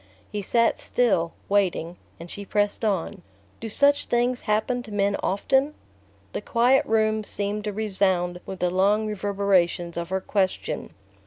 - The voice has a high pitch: Yes, high, 205 Hz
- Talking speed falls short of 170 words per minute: Yes, average, 150 wpm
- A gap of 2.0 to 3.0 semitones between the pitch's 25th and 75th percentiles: Yes, narrow, 2.6 semitones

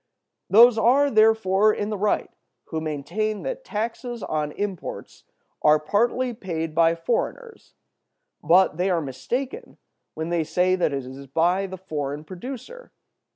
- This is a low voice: No, high, 190 Hz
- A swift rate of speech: No, average, 140 wpm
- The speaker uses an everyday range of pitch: No, wide, 6.2 semitones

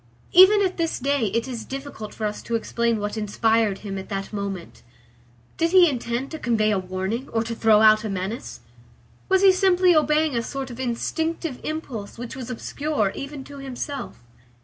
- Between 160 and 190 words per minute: Yes, average, 185 wpm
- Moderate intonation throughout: No, wide, 5.8 semitones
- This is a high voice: Yes, high, 235 Hz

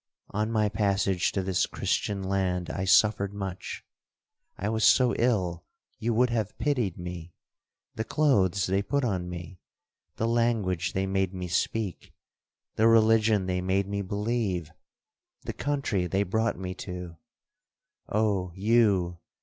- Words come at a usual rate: No, slow, 125 wpm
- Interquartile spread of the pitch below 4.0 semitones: Yes, average, 3.3 semitones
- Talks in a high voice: No, low, 100 Hz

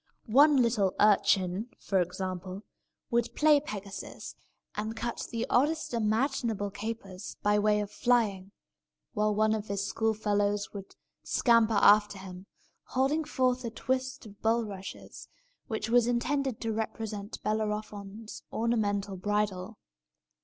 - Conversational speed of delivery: No, slow, 120 wpm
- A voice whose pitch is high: Yes, high, 215 Hz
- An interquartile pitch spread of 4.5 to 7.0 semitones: No, average, 2.7 semitones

